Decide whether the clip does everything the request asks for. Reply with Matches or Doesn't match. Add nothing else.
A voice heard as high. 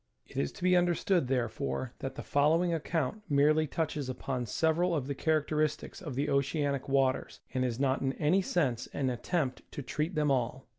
Doesn't match